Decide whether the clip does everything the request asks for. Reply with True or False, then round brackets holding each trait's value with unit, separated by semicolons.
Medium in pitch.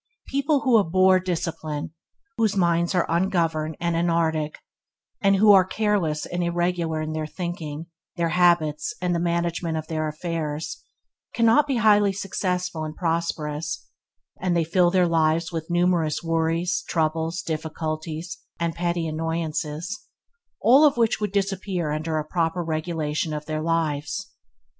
True (170 Hz)